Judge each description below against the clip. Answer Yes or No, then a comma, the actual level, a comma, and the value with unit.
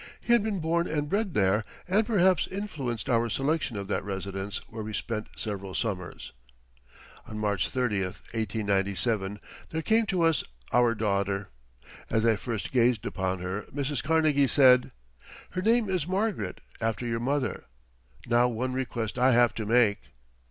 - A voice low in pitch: Yes, low, 120 Hz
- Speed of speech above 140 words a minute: Yes, average, 155 wpm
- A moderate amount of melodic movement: No, wide, 6.9 semitones